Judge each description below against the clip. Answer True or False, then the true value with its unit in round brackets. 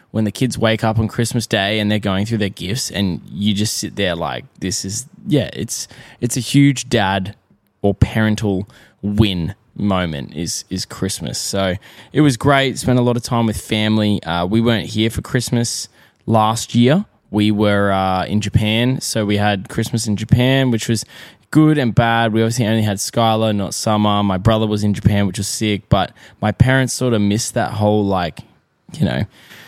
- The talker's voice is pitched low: True (110 Hz)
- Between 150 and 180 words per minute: False (195 wpm)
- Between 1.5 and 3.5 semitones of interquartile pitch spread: True (2.8 semitones)